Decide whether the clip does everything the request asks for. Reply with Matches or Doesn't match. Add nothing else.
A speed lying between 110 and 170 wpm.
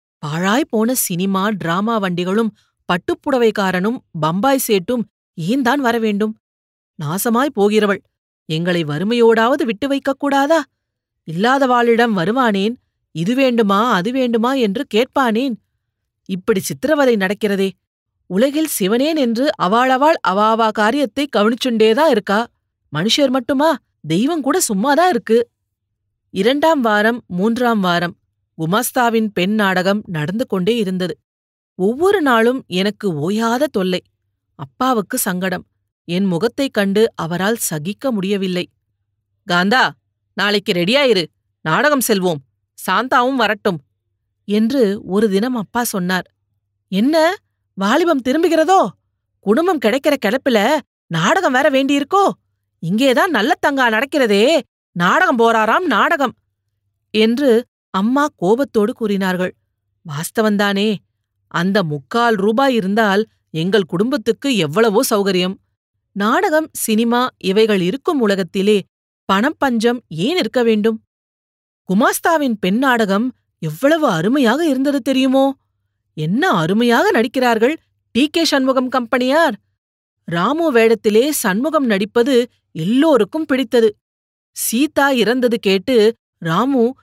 Doesn't match